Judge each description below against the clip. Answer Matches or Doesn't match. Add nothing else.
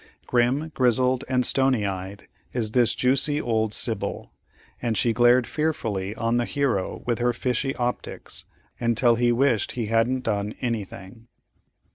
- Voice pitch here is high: Doesn't match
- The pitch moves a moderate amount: Doesn't match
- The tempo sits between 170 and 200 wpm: Doesn't match